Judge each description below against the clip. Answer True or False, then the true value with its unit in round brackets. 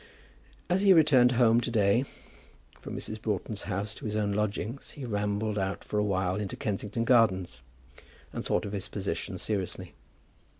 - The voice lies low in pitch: True (105 Hz)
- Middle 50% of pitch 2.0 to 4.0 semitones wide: True (2.7 semitones)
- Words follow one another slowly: False (165 wpm)